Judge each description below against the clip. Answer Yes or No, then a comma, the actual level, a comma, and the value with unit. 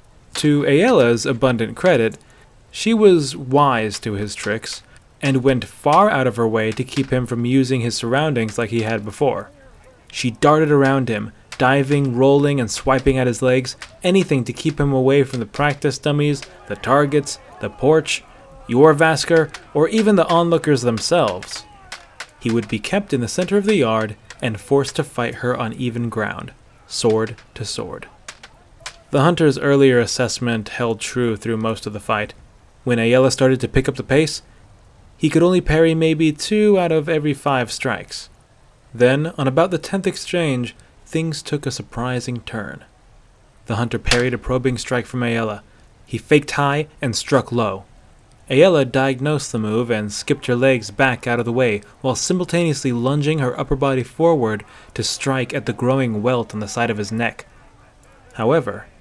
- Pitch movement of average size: Yes, average, 4.0 semitones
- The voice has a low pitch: Yes, low, 130 Hz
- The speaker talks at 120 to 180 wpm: Yes, average, 170 wpm